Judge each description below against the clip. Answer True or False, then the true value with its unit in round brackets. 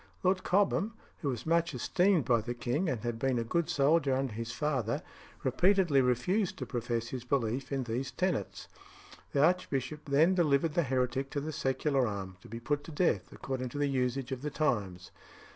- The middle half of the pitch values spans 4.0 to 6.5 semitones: True (4.5 semitones)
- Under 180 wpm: False (190 wpm)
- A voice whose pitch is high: False (135 Hz)